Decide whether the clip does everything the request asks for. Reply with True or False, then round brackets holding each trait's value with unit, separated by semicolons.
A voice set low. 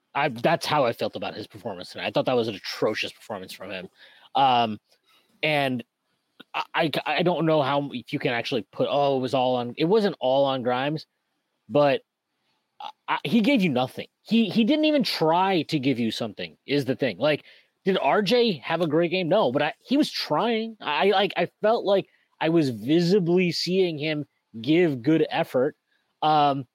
False (155 Hz)